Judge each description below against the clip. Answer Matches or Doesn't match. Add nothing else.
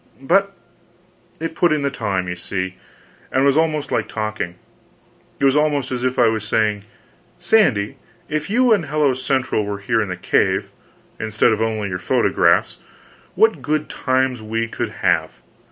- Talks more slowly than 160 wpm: Doesn't match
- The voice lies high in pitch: Doesn't match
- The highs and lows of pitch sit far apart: Matches